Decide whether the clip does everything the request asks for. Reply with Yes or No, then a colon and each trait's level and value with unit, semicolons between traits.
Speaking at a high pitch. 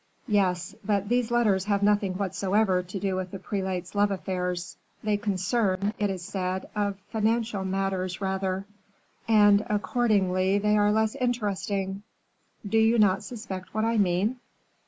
Yes: high, 200 Hz